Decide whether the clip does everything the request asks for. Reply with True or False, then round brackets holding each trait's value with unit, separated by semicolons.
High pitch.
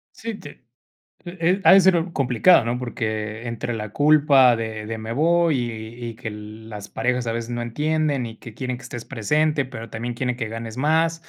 False (120 Hz)